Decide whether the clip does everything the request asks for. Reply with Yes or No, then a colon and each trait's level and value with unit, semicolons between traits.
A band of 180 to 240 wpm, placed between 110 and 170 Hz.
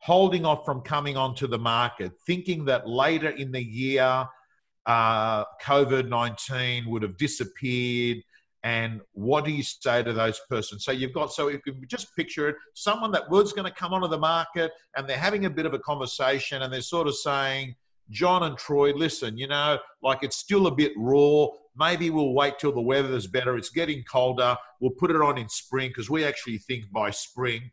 Yes: average, 200 wpm; low, 135 Hz